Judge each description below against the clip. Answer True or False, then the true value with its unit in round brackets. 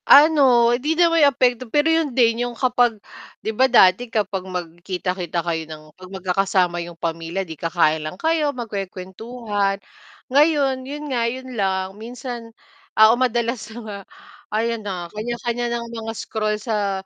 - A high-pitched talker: True (225 Hz)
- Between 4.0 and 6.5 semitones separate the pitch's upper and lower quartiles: True (4.8 semitones)